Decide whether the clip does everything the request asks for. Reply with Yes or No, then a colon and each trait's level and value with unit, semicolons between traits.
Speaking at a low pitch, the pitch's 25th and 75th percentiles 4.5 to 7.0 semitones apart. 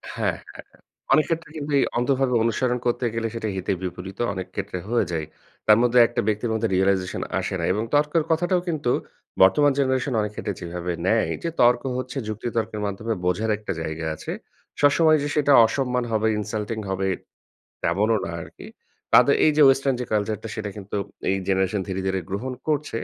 Yes: low, 110 Hz; average, 5.2 semitones